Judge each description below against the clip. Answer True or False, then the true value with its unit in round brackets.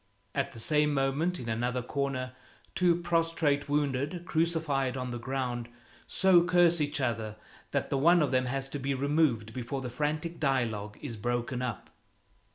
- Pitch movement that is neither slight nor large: True (4.1 semitones)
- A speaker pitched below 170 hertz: True (135 Hz)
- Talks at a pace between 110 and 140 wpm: False (160 wpm)